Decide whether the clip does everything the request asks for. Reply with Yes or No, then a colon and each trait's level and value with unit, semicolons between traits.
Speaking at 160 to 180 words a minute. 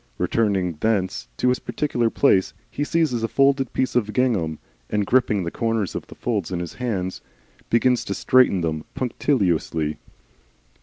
Yes: average, 165 wpm